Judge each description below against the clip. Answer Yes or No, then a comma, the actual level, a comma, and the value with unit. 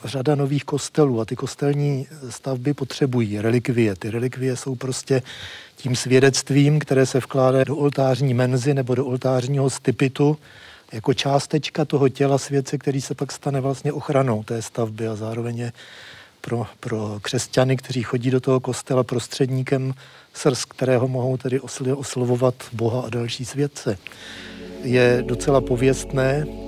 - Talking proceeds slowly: No, average, 135 wpm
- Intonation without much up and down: Yes, narrow, 1.9 semitones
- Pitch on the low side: Yes, low, 130 Hz